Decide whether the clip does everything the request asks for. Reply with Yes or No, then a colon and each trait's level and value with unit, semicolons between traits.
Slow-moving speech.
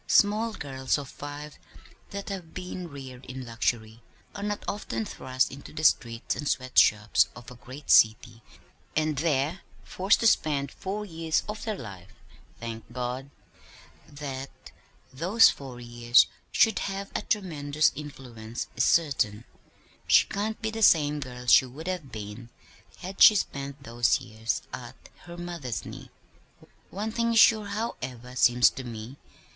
No: average, 150 wpm